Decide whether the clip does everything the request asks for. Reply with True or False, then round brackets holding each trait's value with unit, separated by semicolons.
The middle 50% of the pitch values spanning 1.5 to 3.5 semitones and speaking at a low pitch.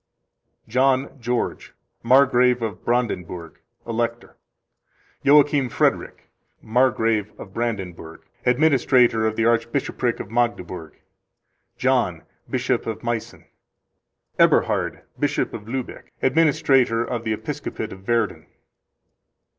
True (2.6 semitones; 120 Hz)